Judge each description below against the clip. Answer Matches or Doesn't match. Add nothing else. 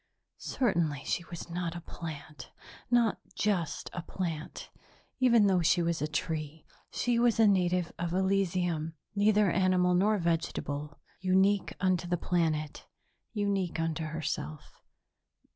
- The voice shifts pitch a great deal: Doesn't match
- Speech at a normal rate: Doesn't match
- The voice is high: Doesn't match